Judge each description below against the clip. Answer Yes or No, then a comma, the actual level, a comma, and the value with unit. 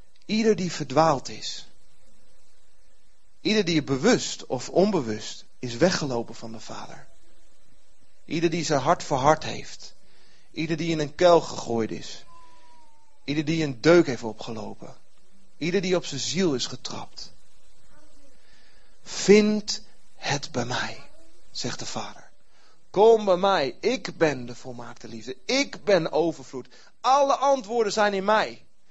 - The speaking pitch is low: No, medium, 165 Hz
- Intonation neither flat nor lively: No, wide, 7.8 semitones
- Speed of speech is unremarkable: No, slow, 130 wpm